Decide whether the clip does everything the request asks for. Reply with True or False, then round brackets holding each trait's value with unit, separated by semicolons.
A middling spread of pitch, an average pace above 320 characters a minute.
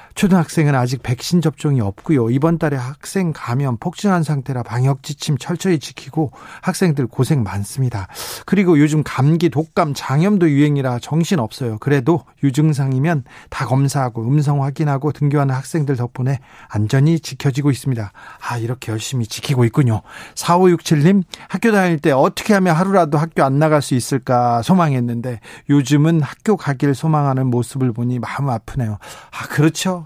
True (4.4 semitones; 355 characters per minute)